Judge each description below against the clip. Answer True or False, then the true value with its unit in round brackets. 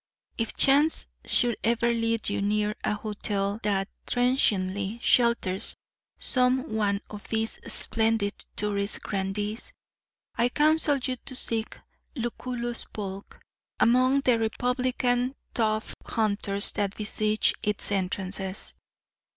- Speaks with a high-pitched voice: True (220 Hz)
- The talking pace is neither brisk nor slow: False (110 wpm)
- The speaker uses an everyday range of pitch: True (3.3 semitones)